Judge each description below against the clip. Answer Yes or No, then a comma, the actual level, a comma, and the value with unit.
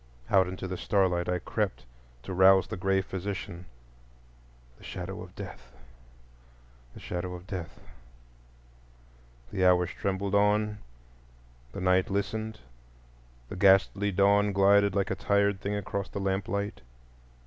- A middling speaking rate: No, slow, 125 wpm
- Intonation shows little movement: Yes, narrow, 2.2 semitones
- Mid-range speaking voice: No, very low, 95 Hz